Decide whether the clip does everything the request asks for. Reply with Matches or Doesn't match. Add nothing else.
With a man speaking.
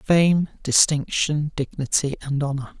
Matches